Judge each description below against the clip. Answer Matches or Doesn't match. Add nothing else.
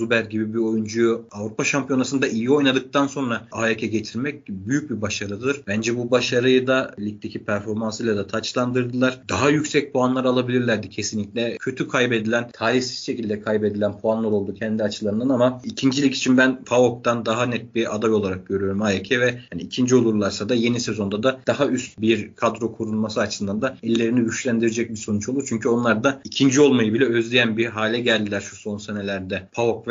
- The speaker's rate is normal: Doesn't match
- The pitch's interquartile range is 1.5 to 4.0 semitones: Matches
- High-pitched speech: Doesn't match